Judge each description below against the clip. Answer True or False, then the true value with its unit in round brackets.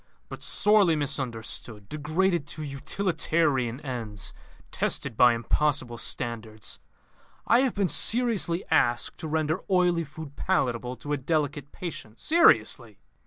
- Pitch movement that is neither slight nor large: False (6.0 semitones)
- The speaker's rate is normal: False (120 wpm)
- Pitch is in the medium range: True (145 Hz)